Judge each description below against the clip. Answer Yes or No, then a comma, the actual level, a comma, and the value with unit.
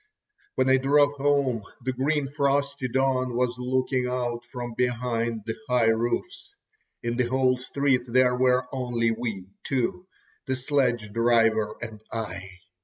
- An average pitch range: No, narrow, 2.2 semitones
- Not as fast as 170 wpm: Yes, average, 140 wpm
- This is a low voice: Yes, low, 125 Hz